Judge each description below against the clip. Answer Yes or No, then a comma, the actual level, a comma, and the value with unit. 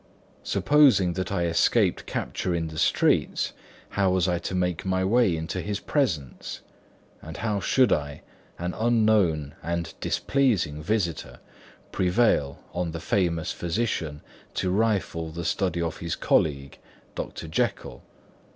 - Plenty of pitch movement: No, average, 3.8 semitones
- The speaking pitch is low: Yes, very low, 90 Hz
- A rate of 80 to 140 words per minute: Yes, slow, 135 wpm